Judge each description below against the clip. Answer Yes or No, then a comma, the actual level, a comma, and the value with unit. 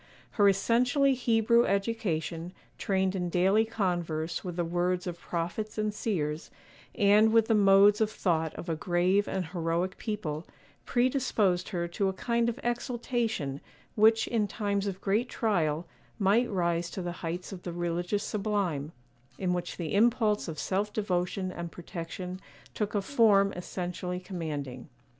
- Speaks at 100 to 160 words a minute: Yes, average, 150 wpm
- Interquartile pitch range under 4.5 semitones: Yes, average, 3.6 semitones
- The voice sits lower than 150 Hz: No, high, 190 Hz